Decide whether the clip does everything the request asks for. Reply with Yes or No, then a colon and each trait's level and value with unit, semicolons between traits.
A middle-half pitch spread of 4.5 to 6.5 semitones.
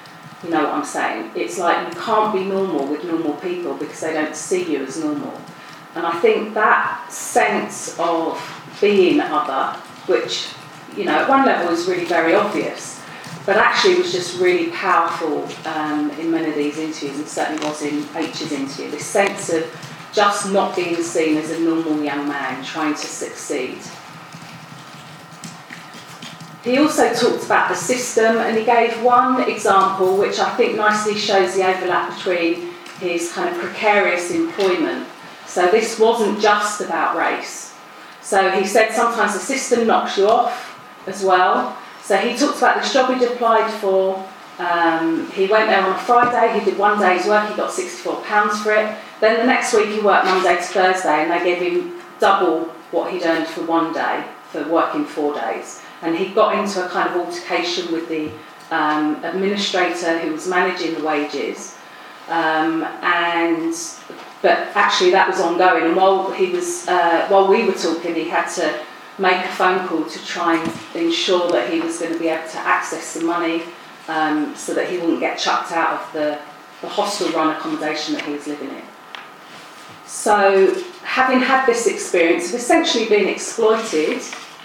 Yes: average, 5.2 semitones